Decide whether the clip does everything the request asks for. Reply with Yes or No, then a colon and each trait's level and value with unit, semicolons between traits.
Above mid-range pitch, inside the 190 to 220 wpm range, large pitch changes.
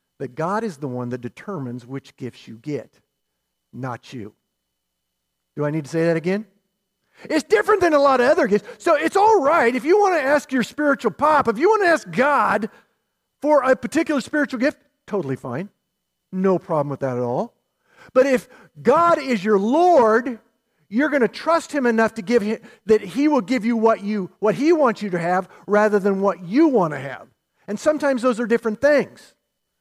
Yes: high, 225 Hz; average, 200 wpm; wide, 7.9 semitones